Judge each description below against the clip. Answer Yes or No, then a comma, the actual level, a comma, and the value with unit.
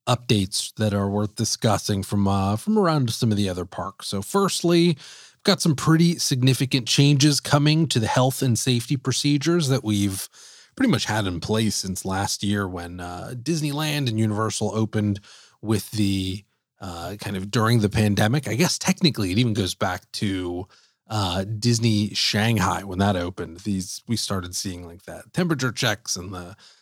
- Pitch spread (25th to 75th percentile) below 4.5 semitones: No, average, 5.2 semitones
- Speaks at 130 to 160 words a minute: No, average, 170 wpm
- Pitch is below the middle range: Yes, low, 110 Hz